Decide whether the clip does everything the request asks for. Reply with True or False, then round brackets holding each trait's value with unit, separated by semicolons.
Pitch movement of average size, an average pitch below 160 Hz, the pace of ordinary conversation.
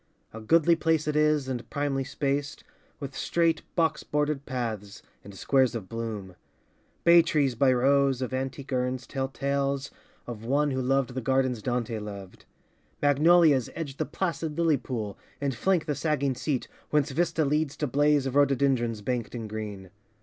True (3.4 semitones; 135 Hz; 165 wpm)